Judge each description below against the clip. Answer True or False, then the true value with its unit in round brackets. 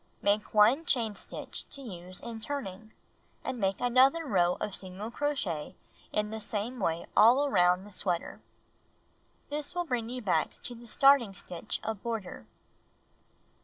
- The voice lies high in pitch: True (220 Hz)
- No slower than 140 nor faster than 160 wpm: True (145 wpm)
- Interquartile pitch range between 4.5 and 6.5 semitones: True (5.0 semitones)